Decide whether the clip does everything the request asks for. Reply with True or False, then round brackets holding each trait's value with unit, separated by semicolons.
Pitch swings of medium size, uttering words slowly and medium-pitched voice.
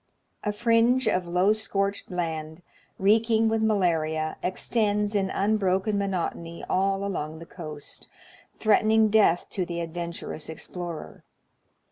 False (4.0 semitones; 120 wpm; 195 Hz)